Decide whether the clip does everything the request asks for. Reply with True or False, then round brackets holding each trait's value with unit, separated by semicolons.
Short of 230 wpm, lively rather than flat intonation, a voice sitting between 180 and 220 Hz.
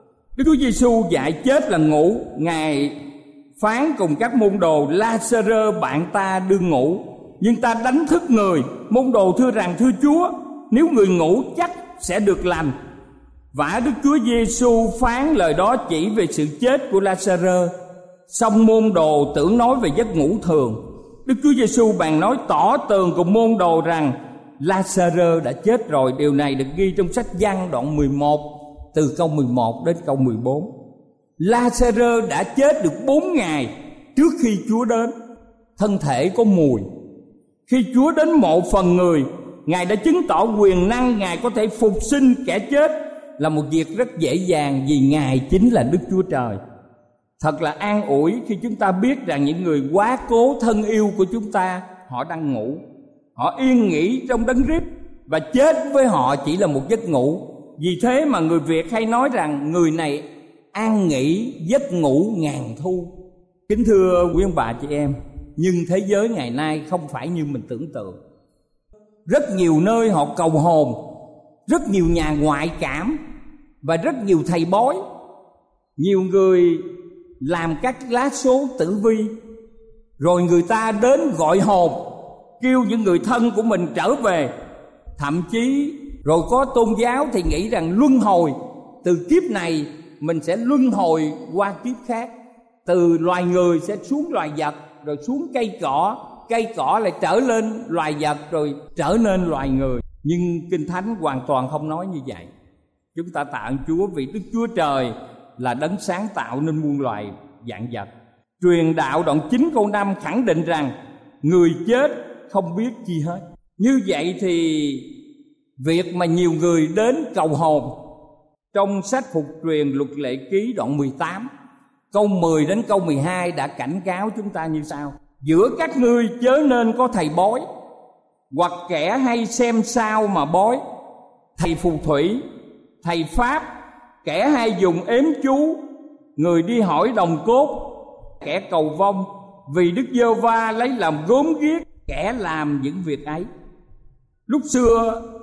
True (170 wpm; 7.5 semitones; 190 Hz)